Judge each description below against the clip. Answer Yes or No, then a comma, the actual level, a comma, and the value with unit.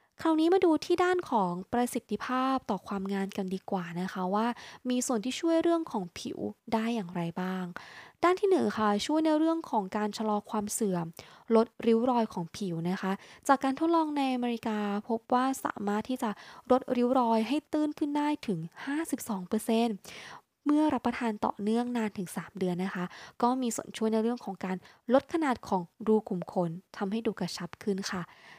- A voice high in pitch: Yes, high, 225 Hz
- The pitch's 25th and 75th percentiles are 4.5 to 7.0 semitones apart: Yes, average, 5.1 semitones